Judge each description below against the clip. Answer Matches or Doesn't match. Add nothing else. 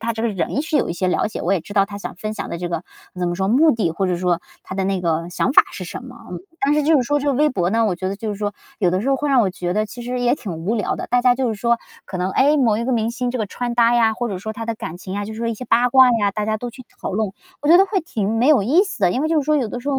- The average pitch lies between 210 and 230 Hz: Matches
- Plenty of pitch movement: Doesn't match